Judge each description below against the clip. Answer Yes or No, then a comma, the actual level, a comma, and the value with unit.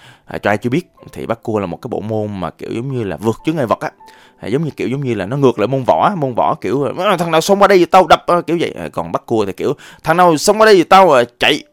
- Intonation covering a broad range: Yes, wide, 8.6 semitones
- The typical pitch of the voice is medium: Yes, medium, 155 Hz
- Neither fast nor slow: No, fast, 310 wpm